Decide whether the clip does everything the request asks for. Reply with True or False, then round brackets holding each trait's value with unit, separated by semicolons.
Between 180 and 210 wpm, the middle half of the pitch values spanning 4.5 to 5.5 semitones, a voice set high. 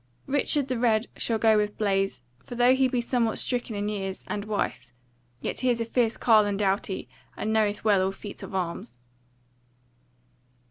False (185 wpm; 3.3 semitones; 215 Hz)